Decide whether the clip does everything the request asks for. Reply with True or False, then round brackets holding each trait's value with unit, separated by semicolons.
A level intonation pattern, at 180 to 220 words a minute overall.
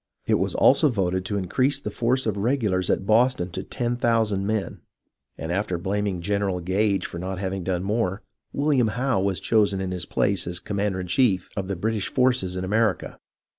False (3.5 semitones; 190 wpm)